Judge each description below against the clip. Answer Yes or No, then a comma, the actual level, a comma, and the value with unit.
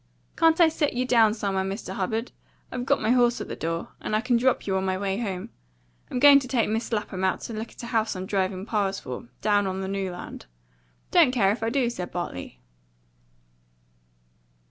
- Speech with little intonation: No, average, 4.3 semitones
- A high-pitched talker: Yes, high, 215 Hz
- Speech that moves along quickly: Yes, fast, 210 wpm